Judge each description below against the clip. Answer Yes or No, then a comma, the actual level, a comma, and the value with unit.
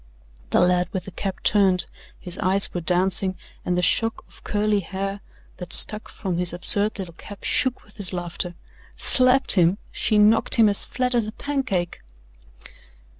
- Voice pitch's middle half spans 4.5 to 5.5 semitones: No, average, 3.0 semitones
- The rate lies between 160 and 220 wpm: Yes, average, 170 wpm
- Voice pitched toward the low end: No, high, 195 Hz